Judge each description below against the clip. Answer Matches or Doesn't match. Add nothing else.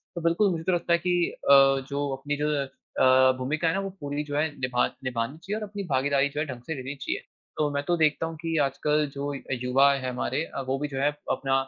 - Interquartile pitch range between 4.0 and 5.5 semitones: Doesn't match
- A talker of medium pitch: Matches